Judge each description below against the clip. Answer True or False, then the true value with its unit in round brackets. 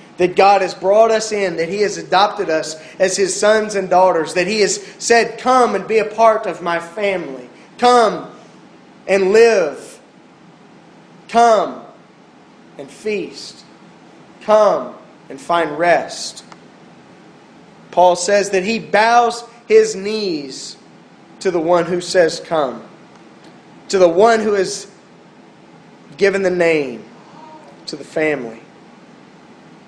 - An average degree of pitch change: True (3.4 semitones)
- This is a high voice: True (195 Hz)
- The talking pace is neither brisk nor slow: False (125 wpm)